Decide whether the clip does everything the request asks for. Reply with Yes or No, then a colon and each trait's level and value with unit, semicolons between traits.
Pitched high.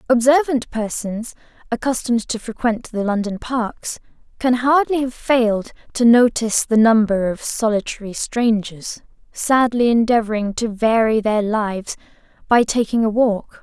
Yes: high, 230 Hz